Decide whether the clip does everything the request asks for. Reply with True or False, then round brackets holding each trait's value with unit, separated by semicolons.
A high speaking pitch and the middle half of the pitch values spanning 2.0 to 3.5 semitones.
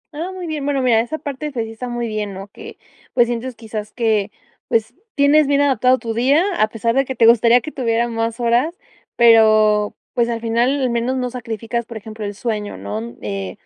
True (235 Hz; 2.9 semitones)